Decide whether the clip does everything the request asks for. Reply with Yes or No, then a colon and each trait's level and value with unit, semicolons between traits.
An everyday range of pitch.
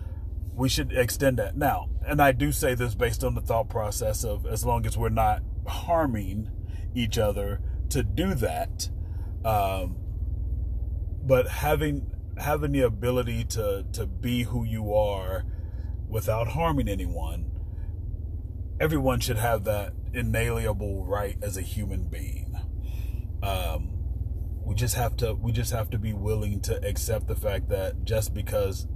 Yes: average, 4.2 semitones